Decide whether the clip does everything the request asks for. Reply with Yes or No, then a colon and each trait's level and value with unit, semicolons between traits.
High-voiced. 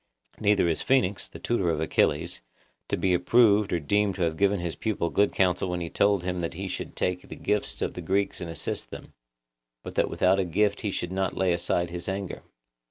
No: very low, 90 Hz